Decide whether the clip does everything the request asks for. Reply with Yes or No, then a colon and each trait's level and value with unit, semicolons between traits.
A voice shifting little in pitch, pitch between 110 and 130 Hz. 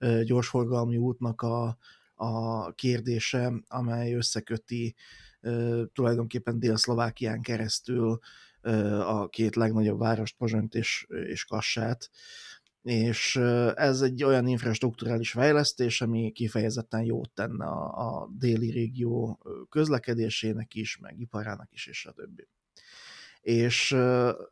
Yes: narrow, 1.4 semitones; low, 115 Hz